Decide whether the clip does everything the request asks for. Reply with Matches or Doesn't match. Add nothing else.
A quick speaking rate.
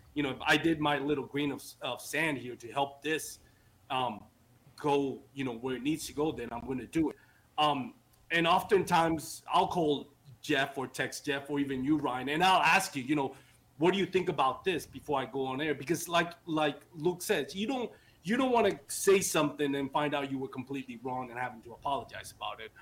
Matches